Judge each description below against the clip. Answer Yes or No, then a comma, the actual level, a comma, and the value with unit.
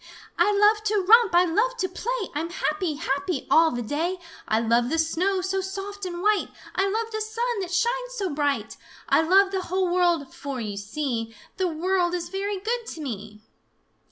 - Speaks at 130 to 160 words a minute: No, average, 190 wpm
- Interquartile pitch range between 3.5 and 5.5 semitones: Yes, average, 4.7 semitones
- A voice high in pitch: Yes, very high, 365 Hz